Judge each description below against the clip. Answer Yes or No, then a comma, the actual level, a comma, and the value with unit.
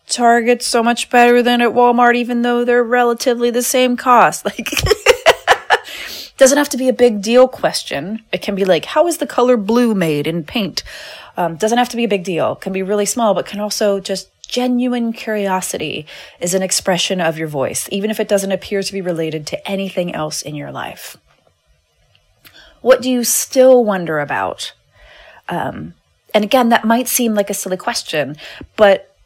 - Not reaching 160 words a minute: No, average, 185 wpm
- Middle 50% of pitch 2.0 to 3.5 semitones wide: No, average, 4.3 semitones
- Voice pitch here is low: No, high, 225 Hz